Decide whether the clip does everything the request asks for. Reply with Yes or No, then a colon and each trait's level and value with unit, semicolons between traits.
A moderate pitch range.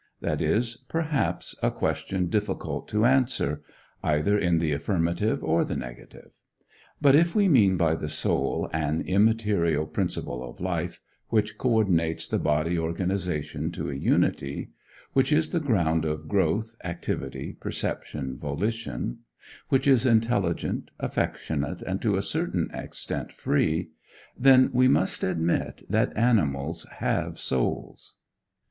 No: wide, 6.6 semitones